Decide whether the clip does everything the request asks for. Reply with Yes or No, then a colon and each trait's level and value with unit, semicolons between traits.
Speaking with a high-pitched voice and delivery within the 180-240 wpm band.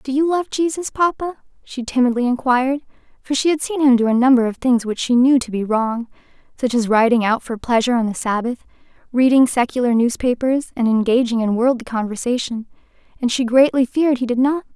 Yes: very high, 250 Hz; average, 185 wpm